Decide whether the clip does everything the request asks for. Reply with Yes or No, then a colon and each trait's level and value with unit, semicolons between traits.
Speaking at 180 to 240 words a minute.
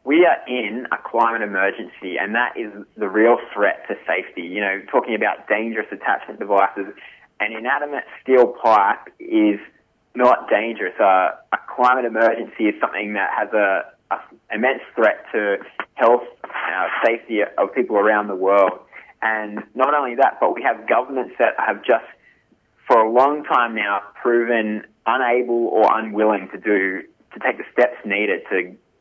No: average, 160 wpm